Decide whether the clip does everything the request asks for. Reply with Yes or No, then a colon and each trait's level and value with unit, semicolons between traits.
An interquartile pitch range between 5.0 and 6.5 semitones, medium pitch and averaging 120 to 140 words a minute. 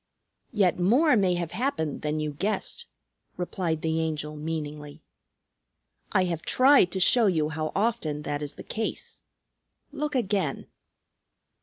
Yes: wide, 5.6 semitones; medium, 170 Hz; slow, 135 wpm